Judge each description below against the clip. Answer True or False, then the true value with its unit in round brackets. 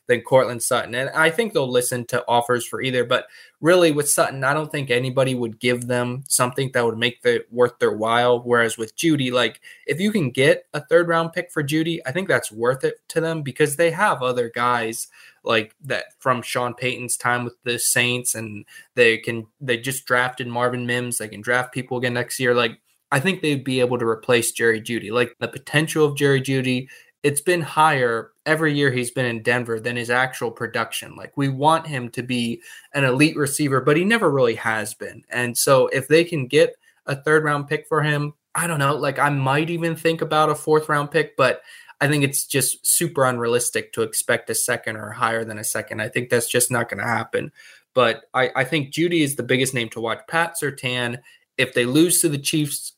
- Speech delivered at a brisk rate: True (220 wpm)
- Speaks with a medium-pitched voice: False (130 Hz)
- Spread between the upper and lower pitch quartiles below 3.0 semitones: False (4.1 semitones)